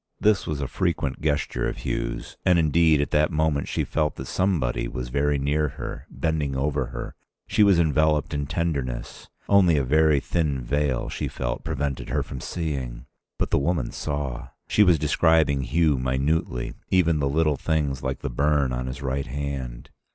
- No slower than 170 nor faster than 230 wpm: Yes, average, 175 wpm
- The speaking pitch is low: Yes, very low, 75 Hz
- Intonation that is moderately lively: Yes, average, 3.0 semitones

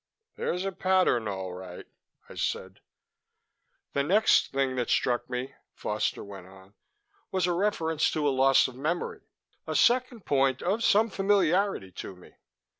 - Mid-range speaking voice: Yes, medium, 145 Hz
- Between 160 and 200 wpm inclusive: No, average, 150 wpm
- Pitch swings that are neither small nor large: No, wide, 8.2 semitones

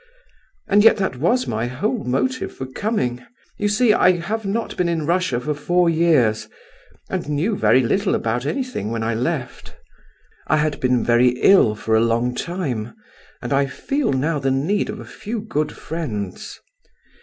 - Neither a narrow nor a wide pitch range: No, wide, 8.0 semitones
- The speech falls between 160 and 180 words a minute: Yes, average, 170 wpm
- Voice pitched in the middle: Yes, medium, 150 Hz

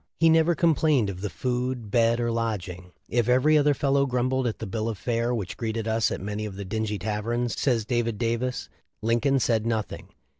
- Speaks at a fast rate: Yes, fast, 210 wpm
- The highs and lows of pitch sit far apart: No, average, 2.9 semitones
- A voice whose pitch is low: Yes, low, 115 Hz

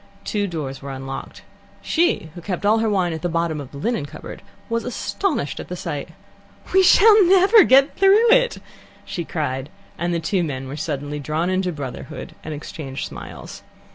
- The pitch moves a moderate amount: No, wide, 8.8 semitones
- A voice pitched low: No, medium, 170 Hz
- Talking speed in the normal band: Yes, average, 180 wpm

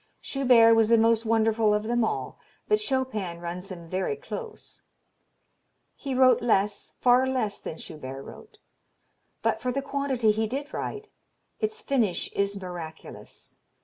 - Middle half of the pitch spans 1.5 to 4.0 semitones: No, average, 4.8 semitones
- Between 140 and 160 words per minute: Yes, average, 145 wpm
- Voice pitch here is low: No, high, 230 Hz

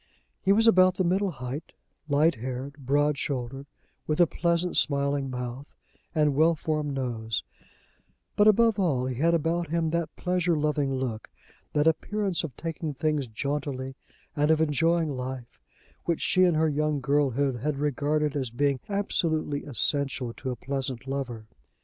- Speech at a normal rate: Yes, average, 155 wpm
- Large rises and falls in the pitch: No, average, 3.7 semitones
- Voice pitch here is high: No, medium, 145 Hz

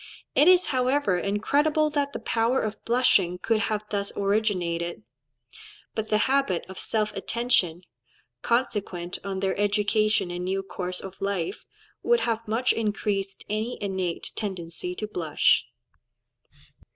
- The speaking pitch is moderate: No, high, 205 Hz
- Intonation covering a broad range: No, average, 3.8 semitones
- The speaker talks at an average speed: No, slow, 130 wpm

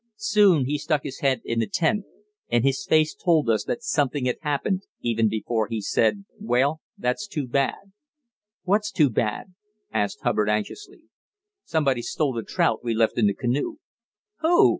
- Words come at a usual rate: Yes, average, 160 wpm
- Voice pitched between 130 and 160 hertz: Yes, medium, 140 Hz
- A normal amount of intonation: No, wide, 7.3 semitones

